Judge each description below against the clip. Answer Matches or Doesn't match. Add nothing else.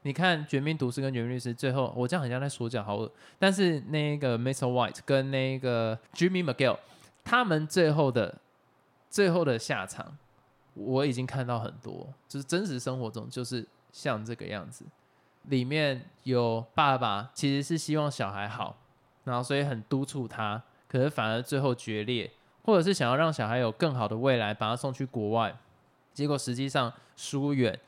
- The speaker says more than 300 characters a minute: Doesn't match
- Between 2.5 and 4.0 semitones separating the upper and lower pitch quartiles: Matches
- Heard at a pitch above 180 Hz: Doesn't match